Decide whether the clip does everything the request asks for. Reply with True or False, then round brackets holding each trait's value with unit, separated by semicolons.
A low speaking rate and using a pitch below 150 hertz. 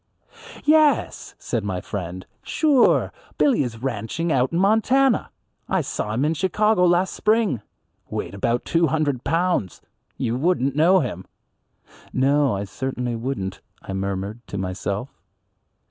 True (130 wpm; 135 Hz)